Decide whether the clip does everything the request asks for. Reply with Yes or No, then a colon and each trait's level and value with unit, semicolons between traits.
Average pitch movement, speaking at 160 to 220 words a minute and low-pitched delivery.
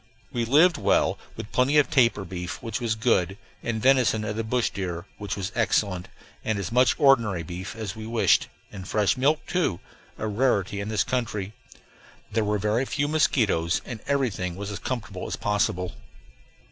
Yes: average, 4.2 semitones; average, 175 wpm; low, 110 Hz